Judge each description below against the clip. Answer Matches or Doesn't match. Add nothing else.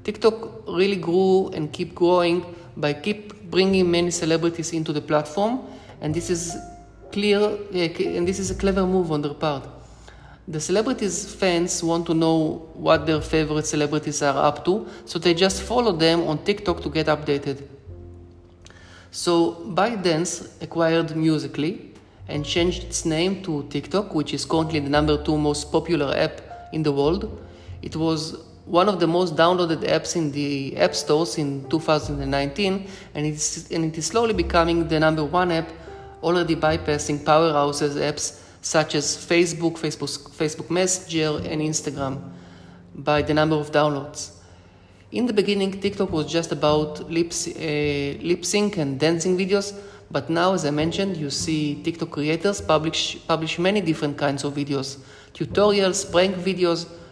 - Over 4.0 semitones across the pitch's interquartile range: Doesn't match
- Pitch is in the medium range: Matches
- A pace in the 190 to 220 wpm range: Doesn't match